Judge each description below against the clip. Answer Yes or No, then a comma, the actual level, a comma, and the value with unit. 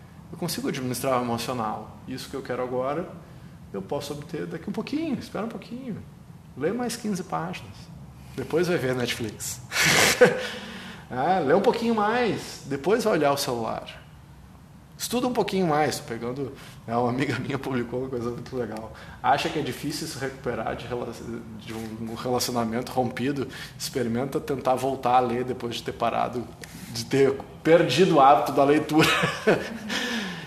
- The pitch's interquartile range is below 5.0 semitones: No, wide, 5.4 semitones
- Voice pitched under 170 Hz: Yes, medium, 140 Hz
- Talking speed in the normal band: Yes, average, 160 wpm